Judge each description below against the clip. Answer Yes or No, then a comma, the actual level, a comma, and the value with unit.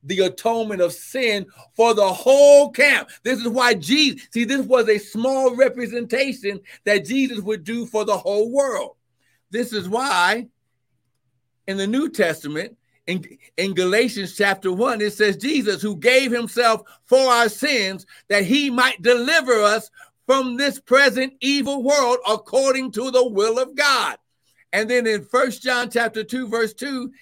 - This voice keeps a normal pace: Yes, average, 160 wpm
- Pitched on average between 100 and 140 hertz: No, high, 235 Hz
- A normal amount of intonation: Yes, average, 4.1 semitones